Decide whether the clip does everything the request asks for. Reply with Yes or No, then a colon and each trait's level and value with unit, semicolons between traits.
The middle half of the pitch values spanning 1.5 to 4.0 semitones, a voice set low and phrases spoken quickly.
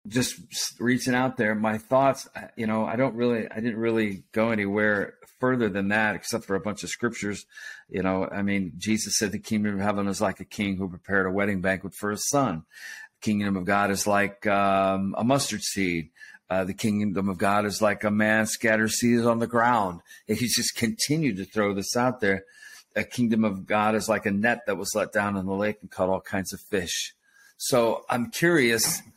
Yes: average, 2.8 semitones; low, 105 Hz; fast, 215 wpm